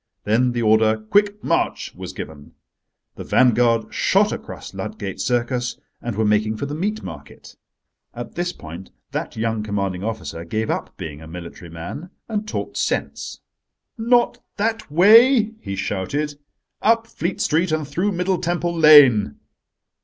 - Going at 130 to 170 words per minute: Yes, average, 145 wpm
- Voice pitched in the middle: No, low, 120 Hz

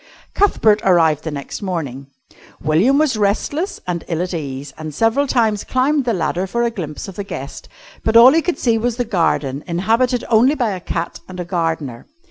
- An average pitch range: No, wide, 6.6 semitones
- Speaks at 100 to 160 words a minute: No, average, 195 wpm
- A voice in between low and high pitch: No, high, 195 Hz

